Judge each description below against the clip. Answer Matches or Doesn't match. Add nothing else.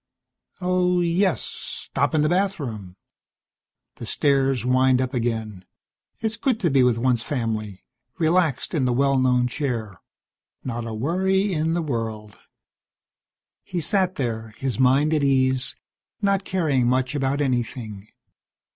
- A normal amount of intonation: Doesn't match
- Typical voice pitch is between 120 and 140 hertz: Matches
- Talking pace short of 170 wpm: Matches